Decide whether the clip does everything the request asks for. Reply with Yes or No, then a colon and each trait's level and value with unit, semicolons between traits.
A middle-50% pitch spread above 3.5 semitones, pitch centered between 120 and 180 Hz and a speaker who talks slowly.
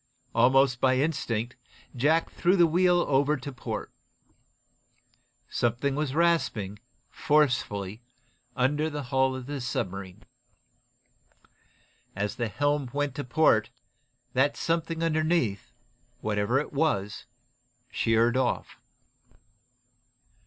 Yes: average, 4.5 semitones; low, 135 Hz; slow, 100 wpm